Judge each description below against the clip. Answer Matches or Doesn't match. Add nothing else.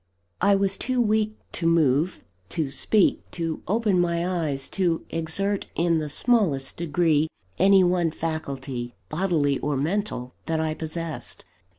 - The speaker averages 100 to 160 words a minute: Matches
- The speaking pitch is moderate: Matches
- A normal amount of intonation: Matches